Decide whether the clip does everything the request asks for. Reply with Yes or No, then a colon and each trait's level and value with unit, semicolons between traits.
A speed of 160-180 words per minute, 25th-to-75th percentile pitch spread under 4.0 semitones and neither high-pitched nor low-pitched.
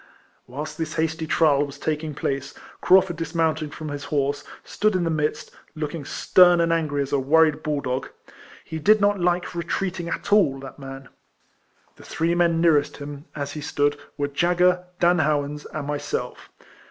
Yes: average, 170 wpm; average, 3.0 semitones; medium, 155 Hz